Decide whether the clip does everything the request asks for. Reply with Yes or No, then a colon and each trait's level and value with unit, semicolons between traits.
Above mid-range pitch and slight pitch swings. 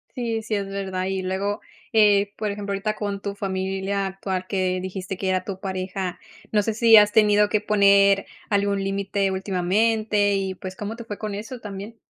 Yes: high, 200 Hz; narrow, 1.6 semitones